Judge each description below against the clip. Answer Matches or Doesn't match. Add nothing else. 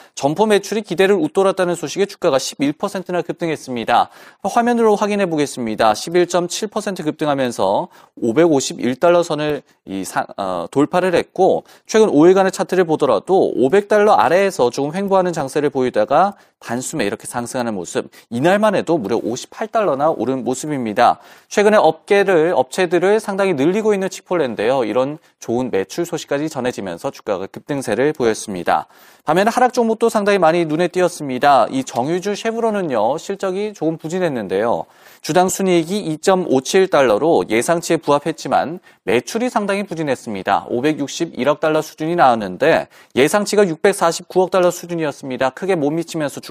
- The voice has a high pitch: Doesn't match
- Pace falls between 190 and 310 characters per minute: Doesn't match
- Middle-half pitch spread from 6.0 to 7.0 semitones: Doesn't match